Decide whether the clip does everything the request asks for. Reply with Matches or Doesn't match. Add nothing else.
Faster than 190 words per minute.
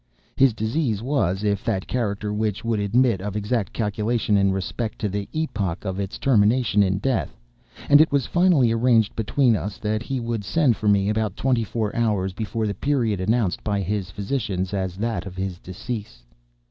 Doesn't match